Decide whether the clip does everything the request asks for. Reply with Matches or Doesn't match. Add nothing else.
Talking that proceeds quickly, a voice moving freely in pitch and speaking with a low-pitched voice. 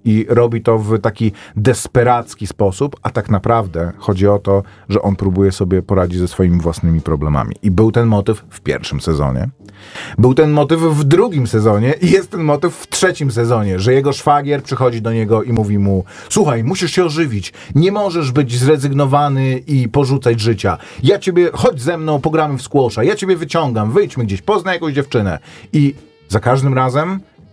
Matches